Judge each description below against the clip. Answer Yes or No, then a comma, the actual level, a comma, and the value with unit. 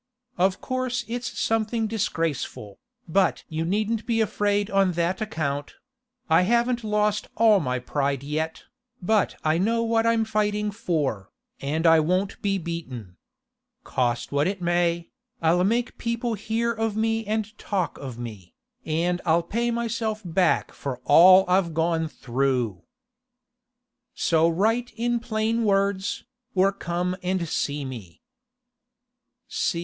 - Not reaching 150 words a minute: Yes, slow, 135 wpm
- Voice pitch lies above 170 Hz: Yes, medium, 185 Hz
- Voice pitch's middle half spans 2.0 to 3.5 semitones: No, wide, 5.6 semitones